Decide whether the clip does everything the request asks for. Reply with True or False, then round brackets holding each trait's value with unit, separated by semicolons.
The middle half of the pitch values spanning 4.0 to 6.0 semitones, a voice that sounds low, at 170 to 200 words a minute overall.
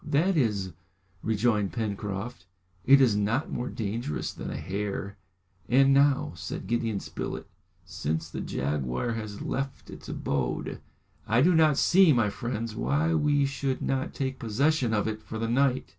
False (5.0 semitones; 115 Hz; 155 wpm)